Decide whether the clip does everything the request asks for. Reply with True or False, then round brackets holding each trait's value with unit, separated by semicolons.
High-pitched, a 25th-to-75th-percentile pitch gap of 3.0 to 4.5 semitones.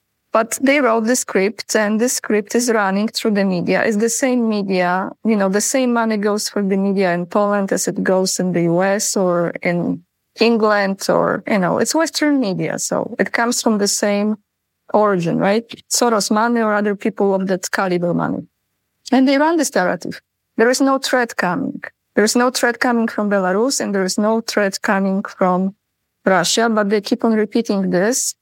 True (215 Hz; 3.3 semitones)